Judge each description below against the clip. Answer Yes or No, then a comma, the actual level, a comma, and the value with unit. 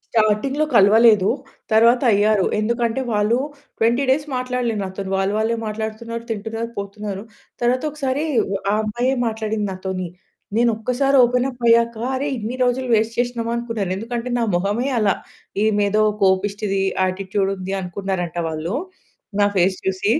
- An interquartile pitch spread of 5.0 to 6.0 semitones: No, average, 3.2 semitones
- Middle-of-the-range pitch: No, high, 220 Hz